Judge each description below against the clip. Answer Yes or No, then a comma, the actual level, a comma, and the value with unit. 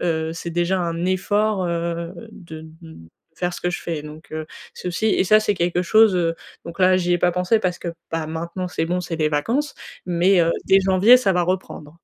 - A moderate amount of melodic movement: No, narrow, 2.0 semitones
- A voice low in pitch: No, medium, 175 Hz